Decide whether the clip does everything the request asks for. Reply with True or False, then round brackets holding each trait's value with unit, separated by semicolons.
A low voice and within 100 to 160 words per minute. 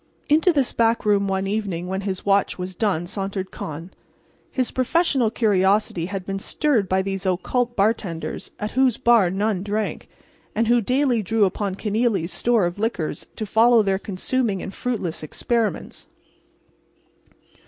False (205 Hz; 150 wpm)